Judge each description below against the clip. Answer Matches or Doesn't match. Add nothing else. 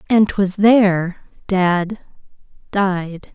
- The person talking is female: Matches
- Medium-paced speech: Doesn't match